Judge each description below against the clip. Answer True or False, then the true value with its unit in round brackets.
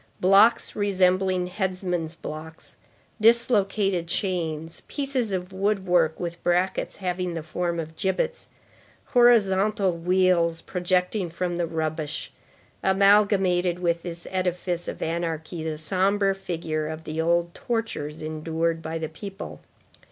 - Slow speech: True (115 wpm)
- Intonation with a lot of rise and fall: False (2.8 semitones)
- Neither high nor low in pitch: True (180 Hz)